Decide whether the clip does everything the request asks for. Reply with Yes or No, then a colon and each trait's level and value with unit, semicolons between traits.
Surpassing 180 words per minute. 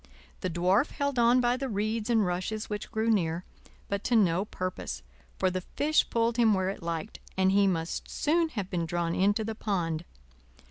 Yes: average, 190 wpm